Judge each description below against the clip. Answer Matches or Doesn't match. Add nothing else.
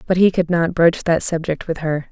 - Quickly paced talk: Matches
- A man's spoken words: Doesn't match